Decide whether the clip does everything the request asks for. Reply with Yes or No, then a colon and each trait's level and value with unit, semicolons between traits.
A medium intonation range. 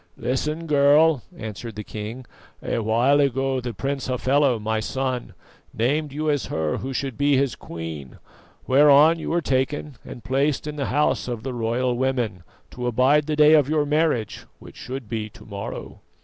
Yes: average, 3.8 semitones